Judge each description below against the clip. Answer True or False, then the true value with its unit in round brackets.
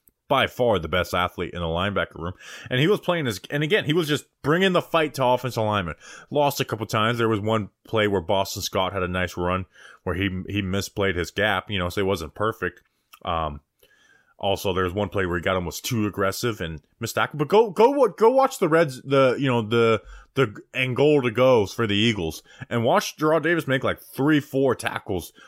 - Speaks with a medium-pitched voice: False (110 Hz)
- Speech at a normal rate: False (225 wpm)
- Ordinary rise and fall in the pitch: False (7.0 semitones)